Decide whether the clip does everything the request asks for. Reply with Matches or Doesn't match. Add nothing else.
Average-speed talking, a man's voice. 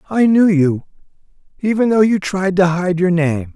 Matches